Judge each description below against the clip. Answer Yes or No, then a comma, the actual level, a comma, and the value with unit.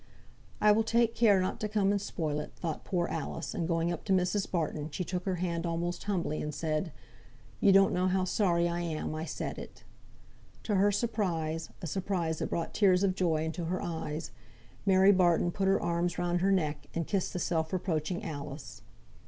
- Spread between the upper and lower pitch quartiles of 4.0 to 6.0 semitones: No, average, 2.9 semitones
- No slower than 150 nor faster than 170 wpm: No, average, 200 wpm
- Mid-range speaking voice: Yes, medium, 175 Hz